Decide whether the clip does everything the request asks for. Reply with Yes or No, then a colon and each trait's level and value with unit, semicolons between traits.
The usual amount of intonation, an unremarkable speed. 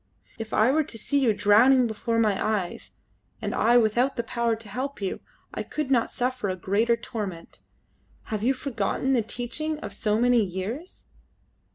Yes: average, 3.4 semitones; average, 175 wpm